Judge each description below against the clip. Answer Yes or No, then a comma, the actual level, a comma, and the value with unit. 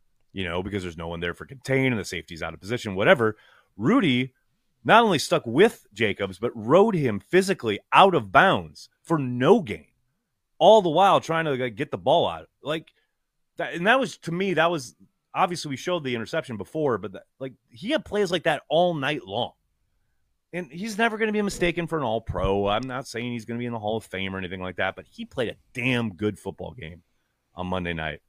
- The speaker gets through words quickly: Yes, fast, 225 wpm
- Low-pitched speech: Yes, low, 120 Hz